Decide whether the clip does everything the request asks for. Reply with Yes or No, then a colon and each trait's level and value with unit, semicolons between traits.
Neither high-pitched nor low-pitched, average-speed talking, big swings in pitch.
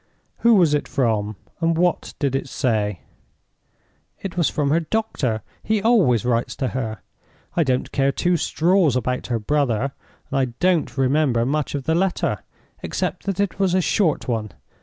Yes: medium, 145 Hz; average, 165 wpm; wide, 5.9 semitones